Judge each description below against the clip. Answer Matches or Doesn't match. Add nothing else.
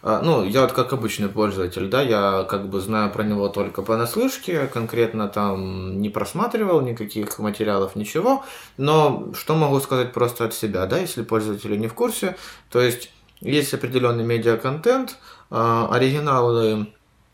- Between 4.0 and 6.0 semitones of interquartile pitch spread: Matches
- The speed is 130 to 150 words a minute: Matches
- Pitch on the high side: Doesn't match